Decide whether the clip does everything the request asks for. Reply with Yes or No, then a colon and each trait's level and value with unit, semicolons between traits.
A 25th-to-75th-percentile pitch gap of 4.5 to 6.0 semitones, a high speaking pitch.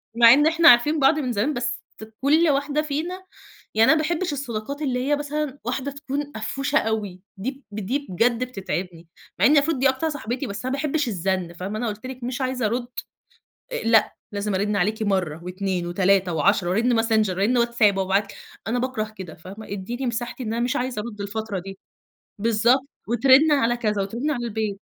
Yes: average, 5.2 semitones; high, 235 Hz